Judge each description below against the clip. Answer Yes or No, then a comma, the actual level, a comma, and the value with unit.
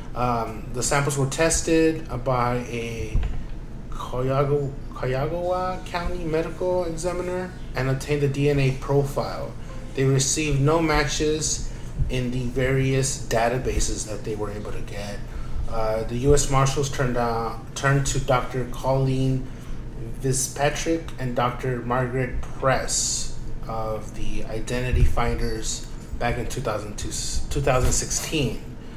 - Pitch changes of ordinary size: Yes, average, 3.4 semitones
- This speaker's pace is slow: Yes, slow, 110 wpm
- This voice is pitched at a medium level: No, low, 130 Hz